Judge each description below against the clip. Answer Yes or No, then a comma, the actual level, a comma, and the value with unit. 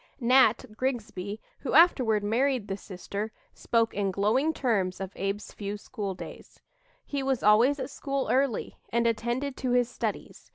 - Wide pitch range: No, average, 4.3 semitones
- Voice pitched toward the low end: No, high, 230 Hz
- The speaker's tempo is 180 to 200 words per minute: No, average, 155 wpm